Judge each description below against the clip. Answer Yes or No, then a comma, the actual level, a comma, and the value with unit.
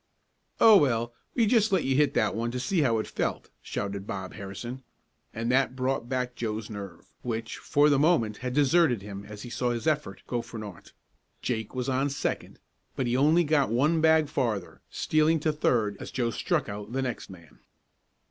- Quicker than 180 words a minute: Yes, average, 195 wpm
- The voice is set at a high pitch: No, low, 125 Hz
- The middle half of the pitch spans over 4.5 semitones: Yes, average, 5.1 semitones